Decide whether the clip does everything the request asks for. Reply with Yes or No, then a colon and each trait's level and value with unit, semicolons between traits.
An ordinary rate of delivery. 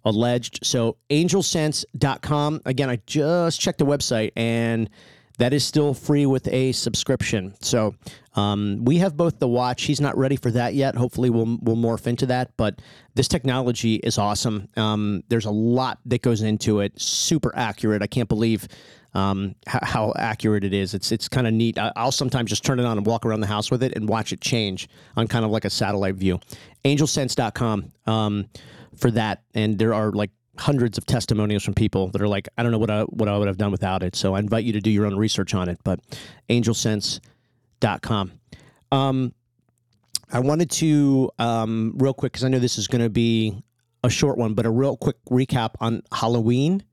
Yes: average, 195 wpm